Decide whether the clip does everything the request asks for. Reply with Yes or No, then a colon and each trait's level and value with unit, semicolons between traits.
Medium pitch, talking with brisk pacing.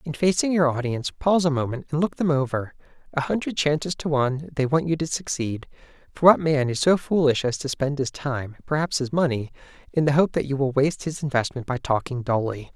Yes: medium, 145 Hz; fast, 215 wpm